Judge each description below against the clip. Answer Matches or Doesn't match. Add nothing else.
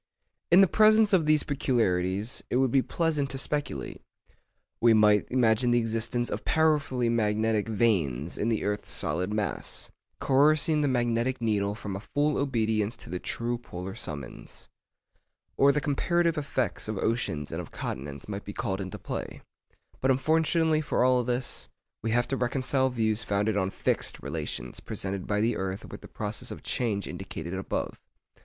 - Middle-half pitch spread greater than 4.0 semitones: Matches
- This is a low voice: Matches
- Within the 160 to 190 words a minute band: Matches